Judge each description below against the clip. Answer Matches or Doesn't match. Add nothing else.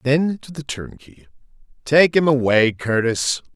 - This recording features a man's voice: Matches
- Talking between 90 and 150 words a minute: Matches